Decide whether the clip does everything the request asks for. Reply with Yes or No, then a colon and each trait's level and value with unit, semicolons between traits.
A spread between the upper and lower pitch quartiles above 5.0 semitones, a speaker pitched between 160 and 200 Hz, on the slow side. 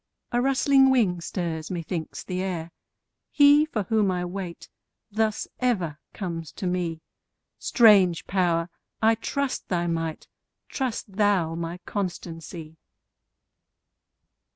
No: average, 4.7 semitones; medium, 185 Hz; slow, 110 wpm